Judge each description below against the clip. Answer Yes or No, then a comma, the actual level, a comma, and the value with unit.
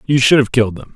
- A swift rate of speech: Yes, fast, 315 wpm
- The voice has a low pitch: Yes, low, 125 Hz